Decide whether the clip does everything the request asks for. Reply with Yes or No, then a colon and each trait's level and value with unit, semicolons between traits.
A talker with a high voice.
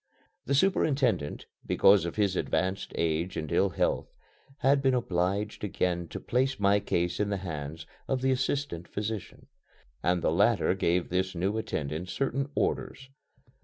No: very low, 95 Hz